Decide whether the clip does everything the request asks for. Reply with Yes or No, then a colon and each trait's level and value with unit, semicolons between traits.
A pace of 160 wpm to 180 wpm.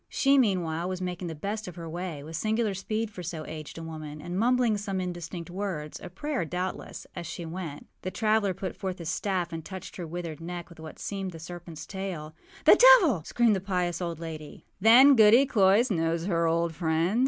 No: average, 200 wpm